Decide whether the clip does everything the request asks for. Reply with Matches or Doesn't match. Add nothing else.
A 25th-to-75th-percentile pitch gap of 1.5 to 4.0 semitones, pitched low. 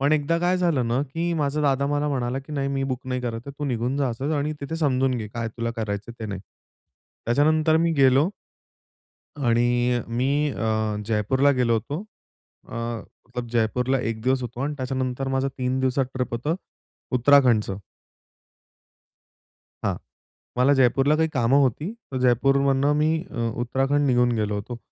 Matches